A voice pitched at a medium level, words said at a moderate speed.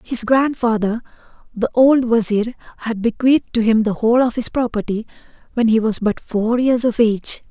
No: high, 230 Hz; average, 175 wpm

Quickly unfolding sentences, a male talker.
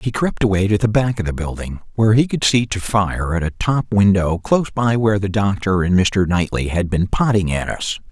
Yes: fast, 235 wpm; male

